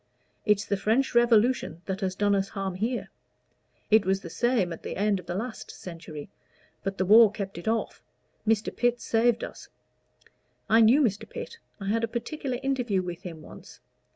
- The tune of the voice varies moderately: Yes, average, 3.7 semitones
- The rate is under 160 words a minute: No, average, 180 wpm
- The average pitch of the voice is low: No, high, 210 Hz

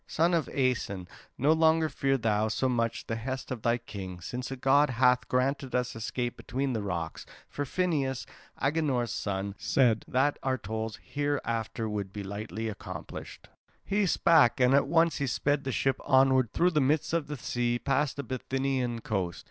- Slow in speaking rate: No, average, 175 wpm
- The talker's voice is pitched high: No, low, 130 Hz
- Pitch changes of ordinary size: Yes, average, 3.9 semitones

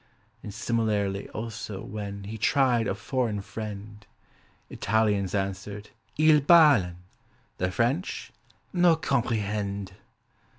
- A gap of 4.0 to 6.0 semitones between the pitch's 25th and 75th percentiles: No, average, 3.2 semitones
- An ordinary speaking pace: No, slow, 95 wpm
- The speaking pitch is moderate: No, low, 105 Hz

